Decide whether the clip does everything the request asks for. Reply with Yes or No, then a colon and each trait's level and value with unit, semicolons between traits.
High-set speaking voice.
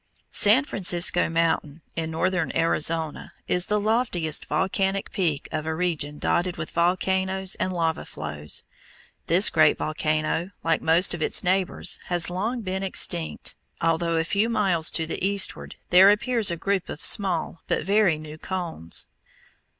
No: medium, 175 Hz